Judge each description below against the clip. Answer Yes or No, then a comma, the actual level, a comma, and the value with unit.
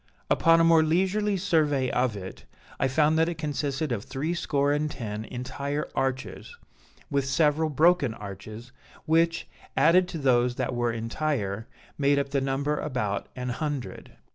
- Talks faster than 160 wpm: No, average, 150 wpm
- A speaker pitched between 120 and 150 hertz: Yes, medium, 140 Hz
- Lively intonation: No, average, 4.2 semitones